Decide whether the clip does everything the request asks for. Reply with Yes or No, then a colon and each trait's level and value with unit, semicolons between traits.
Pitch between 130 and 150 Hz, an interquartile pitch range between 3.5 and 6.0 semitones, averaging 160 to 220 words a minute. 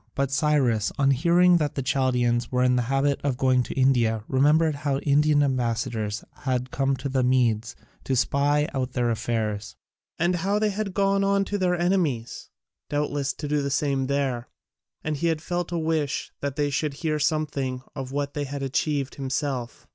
No: medium, 140 Hz; average, 3.1 semitones; average, 180 wpm